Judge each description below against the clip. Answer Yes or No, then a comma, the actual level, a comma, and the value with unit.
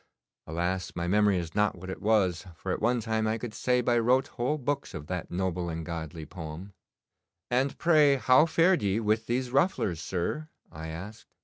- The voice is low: Yes, low, 105 Hz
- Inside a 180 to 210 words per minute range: Yes, average, 190 wpm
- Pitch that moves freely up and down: Yes, wide, 6.1 semitones